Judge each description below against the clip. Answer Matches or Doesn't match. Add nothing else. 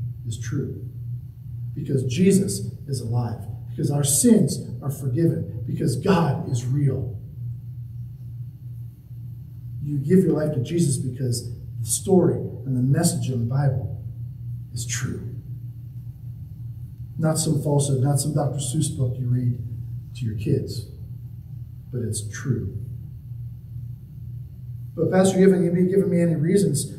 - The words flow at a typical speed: Doesn't match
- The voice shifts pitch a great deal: Doesn't match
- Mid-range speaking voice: Doesn't match